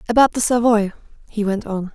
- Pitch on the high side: Yes, high, 215 Hz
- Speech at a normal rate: Yes, average, 185 wpm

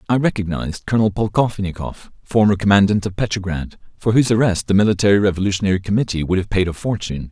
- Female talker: No, male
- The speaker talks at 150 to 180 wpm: Yes, average, 165 wpm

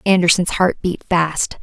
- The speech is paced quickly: No, average, 145 wpm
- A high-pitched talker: No, medium, 180 Hz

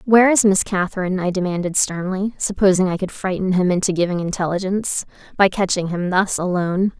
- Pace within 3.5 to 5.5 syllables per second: No, 6.0 syllables/s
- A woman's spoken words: Yes, female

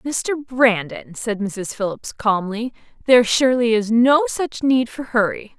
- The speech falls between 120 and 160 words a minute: Yes, average, 150 wpm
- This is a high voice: Yes, high, 235 Hz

